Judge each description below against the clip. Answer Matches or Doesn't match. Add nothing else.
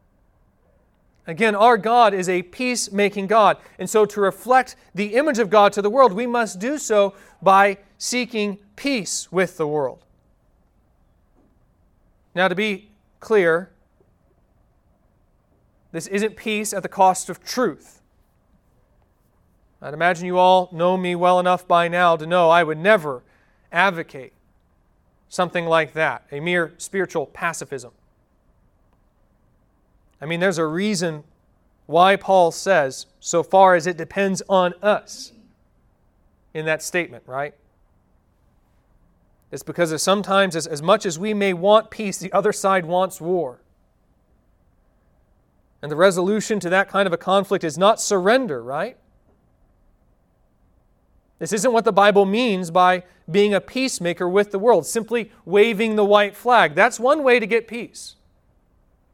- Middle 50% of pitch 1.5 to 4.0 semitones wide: Doesn't match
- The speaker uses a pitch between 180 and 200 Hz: Matches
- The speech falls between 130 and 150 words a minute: Matches